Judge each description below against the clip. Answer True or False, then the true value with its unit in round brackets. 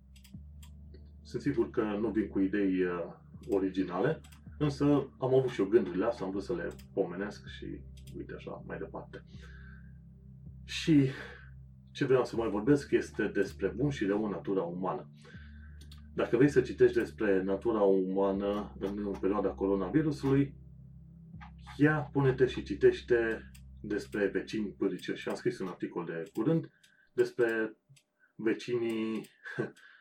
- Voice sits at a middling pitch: False (100 Hz)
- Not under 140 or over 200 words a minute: False (130 wpm)